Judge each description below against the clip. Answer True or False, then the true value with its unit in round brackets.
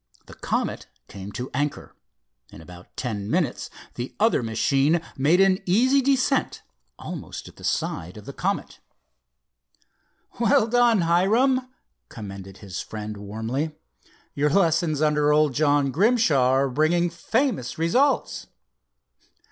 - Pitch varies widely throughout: True (8.3 semitones)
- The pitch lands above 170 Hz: False (150 Hz)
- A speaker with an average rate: False (125 wpm)